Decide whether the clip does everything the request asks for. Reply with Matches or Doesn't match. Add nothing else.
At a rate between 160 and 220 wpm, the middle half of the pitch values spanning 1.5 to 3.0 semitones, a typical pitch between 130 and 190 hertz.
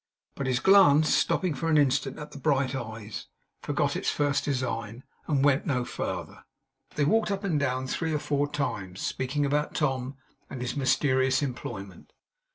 Matches